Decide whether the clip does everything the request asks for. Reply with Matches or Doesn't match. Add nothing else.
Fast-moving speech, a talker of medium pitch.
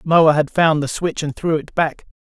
Matches